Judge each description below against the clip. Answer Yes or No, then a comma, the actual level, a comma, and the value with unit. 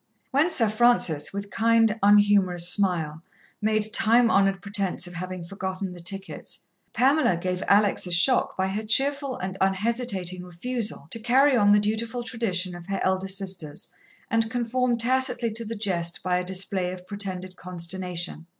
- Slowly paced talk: No, average, 160 wpm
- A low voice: No, high, 200 Hz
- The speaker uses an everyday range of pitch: Yes, average, 4.0 semitones